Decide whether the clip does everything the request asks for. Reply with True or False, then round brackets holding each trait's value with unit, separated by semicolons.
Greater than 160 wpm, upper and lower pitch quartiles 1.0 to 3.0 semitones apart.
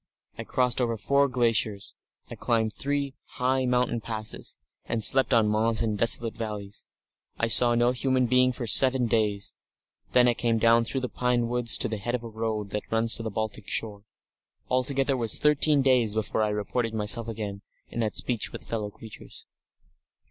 True (180 wpm; 2.5 semitones)